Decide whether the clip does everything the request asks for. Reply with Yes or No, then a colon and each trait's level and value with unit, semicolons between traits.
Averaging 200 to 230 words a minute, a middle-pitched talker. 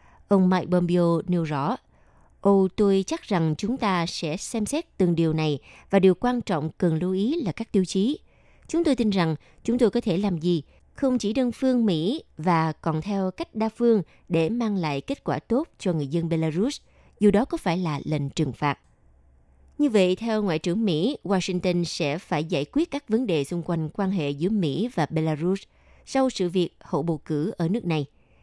Yes: average, 210 wpm; medium, 180 Hz